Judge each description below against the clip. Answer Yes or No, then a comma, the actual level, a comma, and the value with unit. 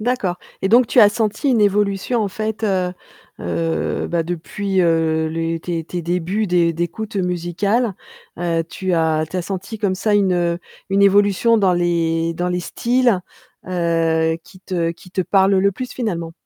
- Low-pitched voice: No, medium, 185 Hz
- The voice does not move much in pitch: No, average, 3.5 semitones